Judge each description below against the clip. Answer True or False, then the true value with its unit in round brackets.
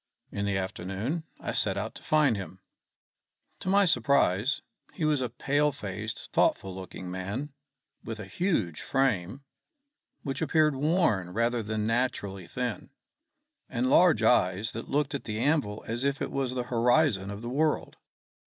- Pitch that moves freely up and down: True (6.0 semitones)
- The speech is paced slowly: False (155 wpm)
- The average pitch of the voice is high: False (120 Hz)